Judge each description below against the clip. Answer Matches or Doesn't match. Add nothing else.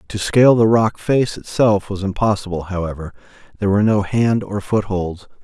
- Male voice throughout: Matches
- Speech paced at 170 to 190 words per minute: Matches